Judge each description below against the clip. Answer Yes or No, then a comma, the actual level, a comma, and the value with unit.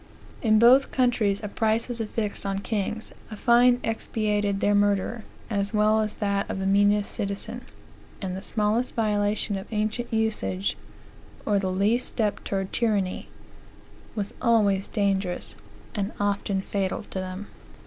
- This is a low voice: No, high, 210 Hz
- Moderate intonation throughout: No, narrow, 2.0 semitones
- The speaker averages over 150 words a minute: No, average, 140 wpm